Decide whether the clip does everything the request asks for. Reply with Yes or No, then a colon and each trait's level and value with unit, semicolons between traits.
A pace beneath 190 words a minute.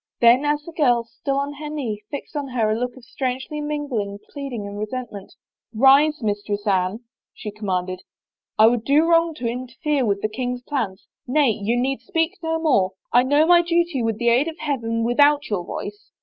No: fast, 205 wpm